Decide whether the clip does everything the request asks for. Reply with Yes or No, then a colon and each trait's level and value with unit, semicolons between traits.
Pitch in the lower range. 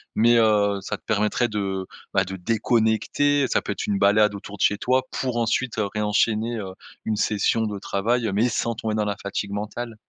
Yes: low, 105 Hz